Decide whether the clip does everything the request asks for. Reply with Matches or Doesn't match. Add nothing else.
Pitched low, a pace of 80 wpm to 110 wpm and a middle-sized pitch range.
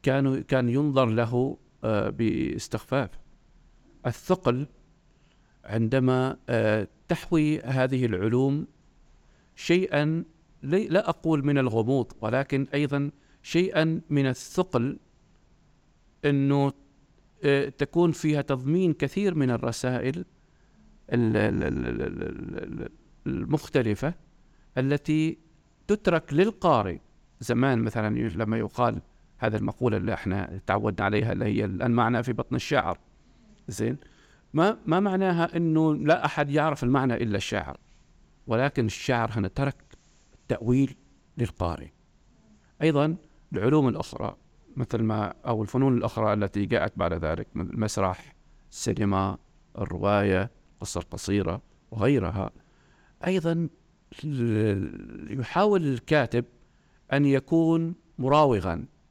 Doesn't match